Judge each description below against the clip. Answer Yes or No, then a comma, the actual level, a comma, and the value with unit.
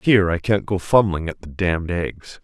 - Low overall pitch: Yes, very low, 90 Hz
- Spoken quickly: Yes, fast, 220 wpm